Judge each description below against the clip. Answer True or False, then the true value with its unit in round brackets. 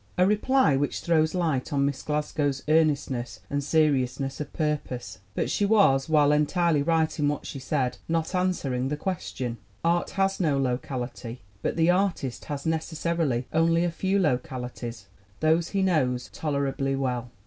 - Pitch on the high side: False (150 Hz)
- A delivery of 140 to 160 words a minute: True (155 wpm)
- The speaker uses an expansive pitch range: False (4.0 semitones)